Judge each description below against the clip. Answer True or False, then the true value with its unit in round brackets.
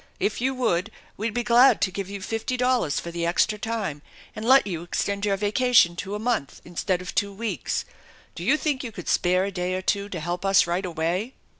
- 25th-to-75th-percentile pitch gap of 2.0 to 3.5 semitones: False (4.3 semitones)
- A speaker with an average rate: False (225 wpm)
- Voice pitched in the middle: False (200 Hz)